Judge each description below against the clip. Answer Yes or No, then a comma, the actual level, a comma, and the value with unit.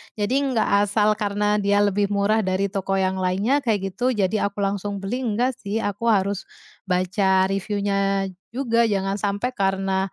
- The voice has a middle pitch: No, high, 200 Hz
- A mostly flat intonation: Yes, narrow, 1.7 semitones